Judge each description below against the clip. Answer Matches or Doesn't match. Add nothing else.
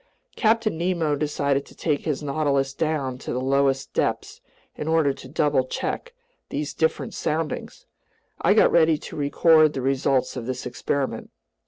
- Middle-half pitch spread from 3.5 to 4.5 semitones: Doesn't match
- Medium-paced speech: Matches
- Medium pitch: Matches